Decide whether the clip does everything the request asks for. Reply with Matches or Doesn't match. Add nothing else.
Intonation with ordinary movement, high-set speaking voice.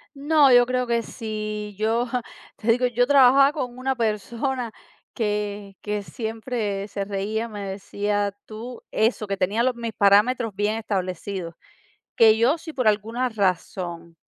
Matches